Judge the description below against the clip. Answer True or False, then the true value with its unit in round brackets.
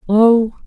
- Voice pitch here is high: True (220 Hz)